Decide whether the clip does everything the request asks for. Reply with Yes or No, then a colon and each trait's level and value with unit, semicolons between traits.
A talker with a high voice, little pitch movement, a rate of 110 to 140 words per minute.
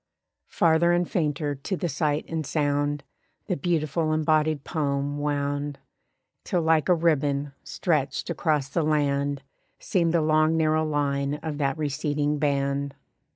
No: medium, 150 Hz; narrow, 1.9 semitones; slow, 135 wpm